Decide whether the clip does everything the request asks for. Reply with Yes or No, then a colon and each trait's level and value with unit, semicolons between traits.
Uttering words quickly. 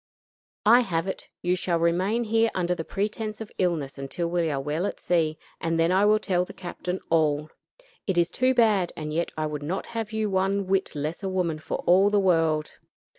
Yes: fast, 210 wpm